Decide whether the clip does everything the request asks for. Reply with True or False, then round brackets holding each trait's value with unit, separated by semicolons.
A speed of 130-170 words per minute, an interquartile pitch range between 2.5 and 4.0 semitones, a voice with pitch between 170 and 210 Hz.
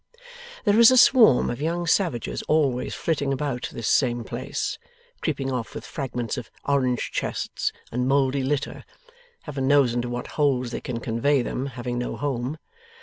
False (160 wpm; 3.1 semitones; 135 Hz)